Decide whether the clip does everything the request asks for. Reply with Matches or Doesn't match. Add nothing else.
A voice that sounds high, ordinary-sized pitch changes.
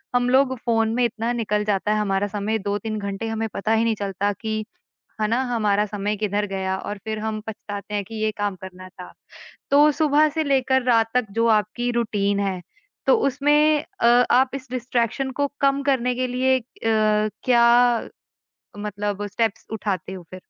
Matches